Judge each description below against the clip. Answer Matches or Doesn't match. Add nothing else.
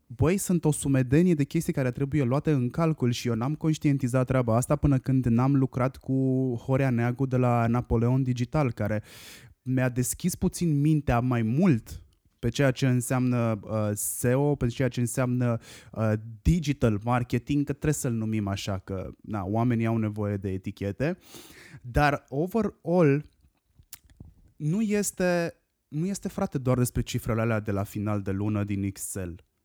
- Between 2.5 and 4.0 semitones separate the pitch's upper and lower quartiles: Doesn't match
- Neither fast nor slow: Matches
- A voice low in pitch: Matches